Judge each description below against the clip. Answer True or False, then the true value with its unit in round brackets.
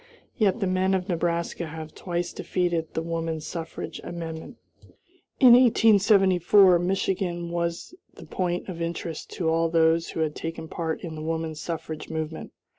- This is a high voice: False (170 Hz)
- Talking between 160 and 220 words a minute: False (150 wpm)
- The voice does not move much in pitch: True (2.2 semitones)